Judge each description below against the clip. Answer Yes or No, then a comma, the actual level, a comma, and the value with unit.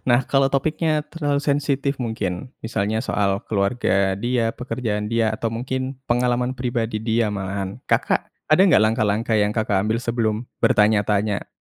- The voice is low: Yes, low, 115 Hz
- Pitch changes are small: No, average, 3.4 semitones